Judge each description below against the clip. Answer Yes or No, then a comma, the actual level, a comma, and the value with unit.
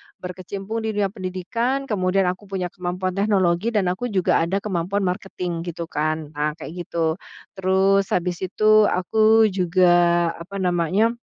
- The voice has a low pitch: No, medium, 185 Hz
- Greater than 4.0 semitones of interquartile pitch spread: No, narrow, 2.5 semitones